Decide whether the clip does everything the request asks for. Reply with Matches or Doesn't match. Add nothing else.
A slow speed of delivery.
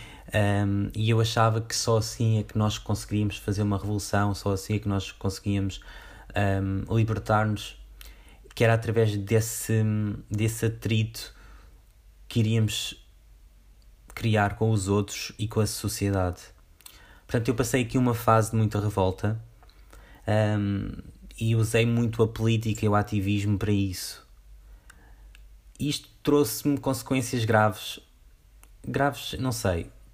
Doesn't match